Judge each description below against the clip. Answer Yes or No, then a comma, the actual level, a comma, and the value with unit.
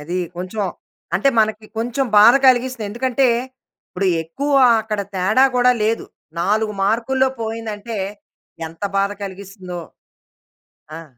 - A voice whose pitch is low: No, high, 215 Hz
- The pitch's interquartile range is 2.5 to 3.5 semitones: No, average, 4.0 semitones